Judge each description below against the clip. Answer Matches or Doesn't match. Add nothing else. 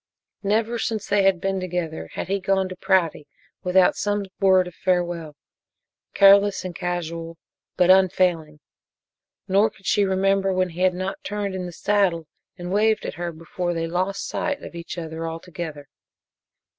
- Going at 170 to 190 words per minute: Doesn't match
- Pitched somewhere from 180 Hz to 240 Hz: Matches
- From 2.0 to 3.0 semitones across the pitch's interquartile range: Matches